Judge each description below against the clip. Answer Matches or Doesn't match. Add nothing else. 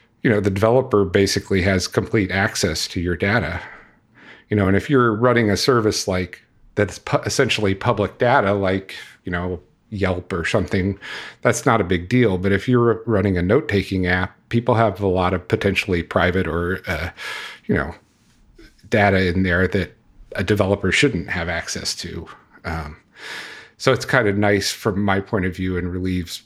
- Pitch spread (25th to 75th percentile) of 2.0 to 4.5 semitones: Matches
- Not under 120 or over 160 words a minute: Doesn't match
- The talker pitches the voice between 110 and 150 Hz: Doesn't match